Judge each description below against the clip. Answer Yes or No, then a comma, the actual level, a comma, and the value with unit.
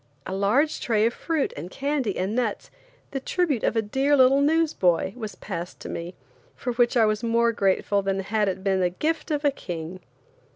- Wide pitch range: Yes, wide, 6.1 semitones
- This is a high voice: Yes, high, 225 Hz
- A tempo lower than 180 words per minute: No, average, 200 wpm